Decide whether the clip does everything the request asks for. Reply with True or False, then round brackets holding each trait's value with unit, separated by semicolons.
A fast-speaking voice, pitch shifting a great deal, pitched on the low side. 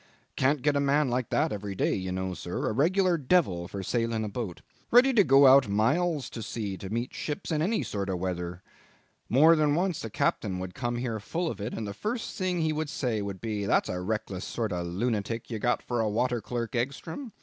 True (230 wpm; 6.8 semitones; 120 Hz)